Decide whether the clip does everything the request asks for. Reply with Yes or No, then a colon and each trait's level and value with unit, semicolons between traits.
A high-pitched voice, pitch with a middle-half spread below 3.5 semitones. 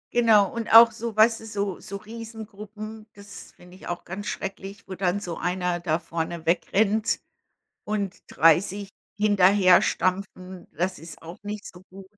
Yes: high, 195 Hz; average, 2.9 semitones